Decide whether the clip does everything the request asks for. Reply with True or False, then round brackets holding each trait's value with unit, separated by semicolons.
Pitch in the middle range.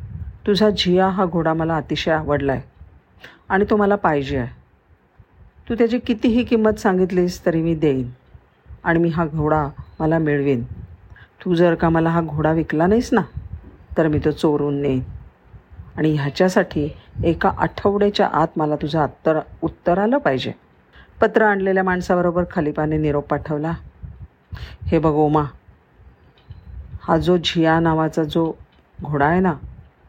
True (160 Hz)